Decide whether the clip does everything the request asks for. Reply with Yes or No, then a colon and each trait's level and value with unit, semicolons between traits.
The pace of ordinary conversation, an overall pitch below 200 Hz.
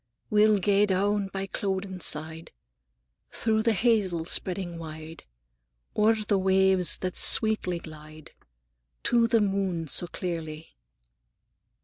No: slow, 110 wpm; high, 190 Hz